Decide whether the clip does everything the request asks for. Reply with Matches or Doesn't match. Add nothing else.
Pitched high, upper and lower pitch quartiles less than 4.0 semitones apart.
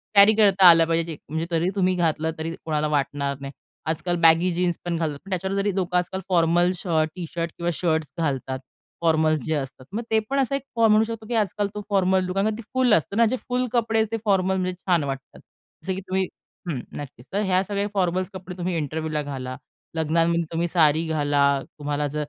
Doesn't match